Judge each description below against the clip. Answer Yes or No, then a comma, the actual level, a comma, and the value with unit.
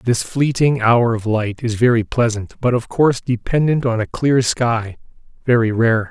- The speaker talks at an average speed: Yes, average, 175 wpm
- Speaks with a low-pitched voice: Yes, low, 120 Hz